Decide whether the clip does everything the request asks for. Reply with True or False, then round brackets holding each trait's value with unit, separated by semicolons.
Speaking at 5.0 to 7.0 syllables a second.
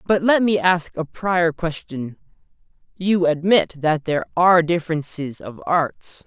False (4.2 syllables/s)